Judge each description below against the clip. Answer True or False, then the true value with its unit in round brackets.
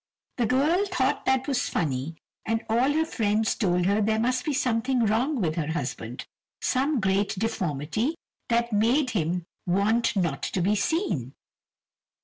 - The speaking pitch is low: False (225 Hz)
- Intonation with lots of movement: True (5.7 semitones)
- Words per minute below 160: True (150 wpm)